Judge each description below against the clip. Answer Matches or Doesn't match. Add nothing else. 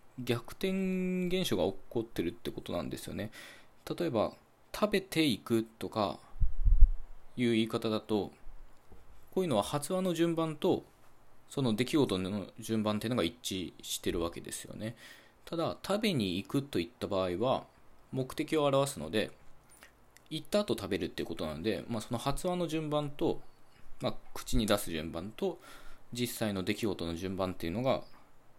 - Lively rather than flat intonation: Matches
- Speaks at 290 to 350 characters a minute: Matches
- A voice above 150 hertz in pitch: Doesn't match